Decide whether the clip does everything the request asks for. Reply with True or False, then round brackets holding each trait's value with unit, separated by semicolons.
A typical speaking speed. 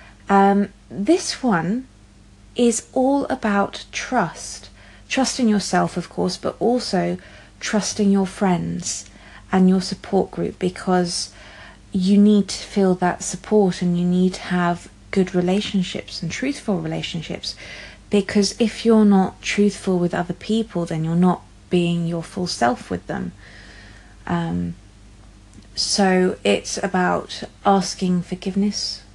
False (125 wpm)